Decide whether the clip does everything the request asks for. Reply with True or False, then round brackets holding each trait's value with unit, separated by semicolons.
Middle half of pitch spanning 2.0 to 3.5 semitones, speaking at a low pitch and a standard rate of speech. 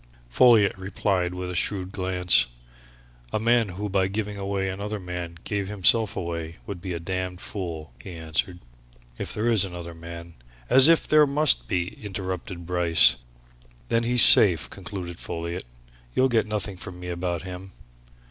True (3.0 semitones; 95 Hz; 160 wpm)